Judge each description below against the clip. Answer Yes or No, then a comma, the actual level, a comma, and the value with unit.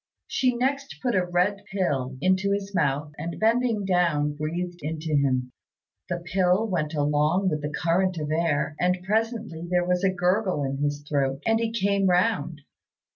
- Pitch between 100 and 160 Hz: No, medium, 180 Hz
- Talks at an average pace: Yes, average, 170 wpm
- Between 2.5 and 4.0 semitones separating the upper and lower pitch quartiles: No, average, 4.9 semitones